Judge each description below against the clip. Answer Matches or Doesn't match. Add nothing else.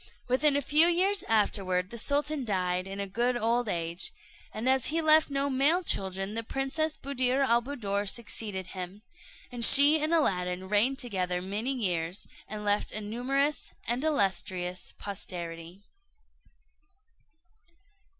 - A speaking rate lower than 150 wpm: Matches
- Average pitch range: Doesn't match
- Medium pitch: Doesn't match